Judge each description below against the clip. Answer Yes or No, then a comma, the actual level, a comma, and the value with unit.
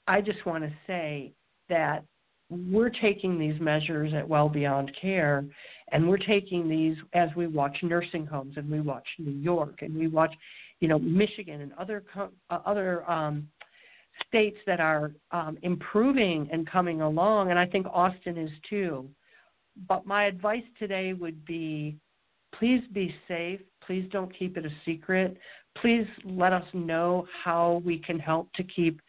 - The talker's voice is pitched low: No, medium, 175 Hz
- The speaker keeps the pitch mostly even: No, average, 3.3 semitones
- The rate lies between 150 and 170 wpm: Yes, average, 160 wpm